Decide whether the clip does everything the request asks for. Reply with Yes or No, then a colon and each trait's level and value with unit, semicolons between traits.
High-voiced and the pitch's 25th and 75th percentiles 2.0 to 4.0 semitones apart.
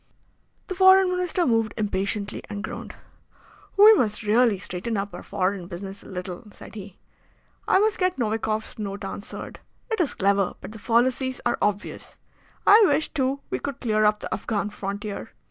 No: high, 215 Hz; average, 4.9 semitones